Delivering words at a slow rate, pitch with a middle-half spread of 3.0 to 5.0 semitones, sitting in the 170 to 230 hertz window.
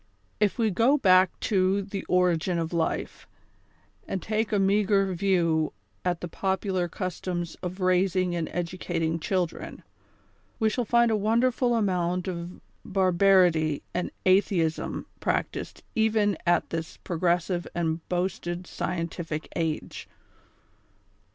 No: slow, 125 wpm; narrow, 2.5 semitones; medium, 185 Hz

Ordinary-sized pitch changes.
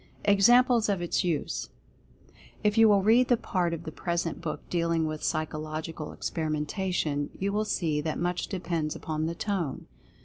Yes: average, 4.2 semitones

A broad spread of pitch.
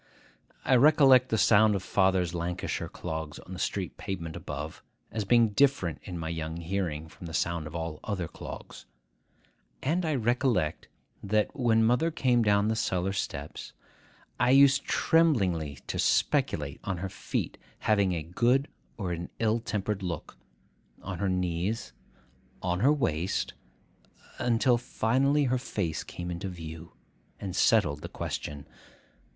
Yes: wide, 6.1 semitones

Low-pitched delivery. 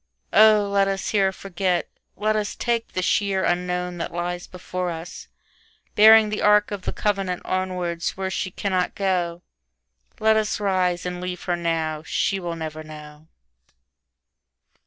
No: medium, 180 Hz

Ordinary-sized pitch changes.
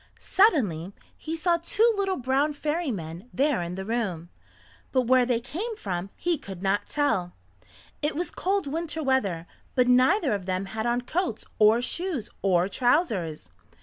No: wide, 8.8 semitones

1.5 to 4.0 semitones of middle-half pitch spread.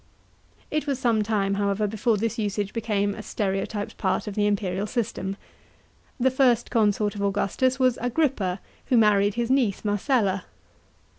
Yes: average, 3.0 semitones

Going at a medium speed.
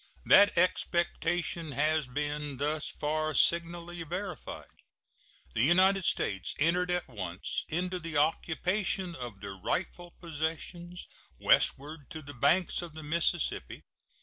No: slow, 120 wpm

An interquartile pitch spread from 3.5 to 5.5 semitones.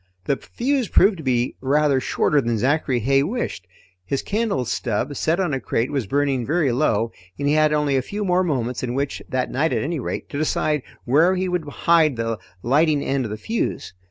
Yes: average, 4.2 semitones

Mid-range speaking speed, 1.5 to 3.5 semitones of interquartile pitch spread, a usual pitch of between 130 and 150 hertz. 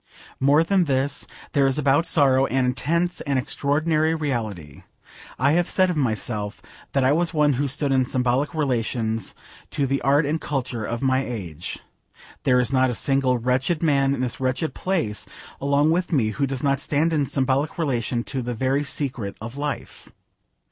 Yes: average, 175 wpm; average, 2.9 semitones; low, 135 Hz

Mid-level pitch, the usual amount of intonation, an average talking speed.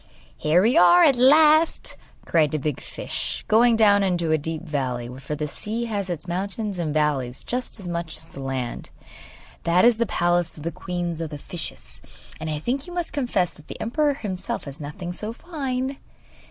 No: medium, 175 Hz; wide, 7.2 semitones; average, 195 wpm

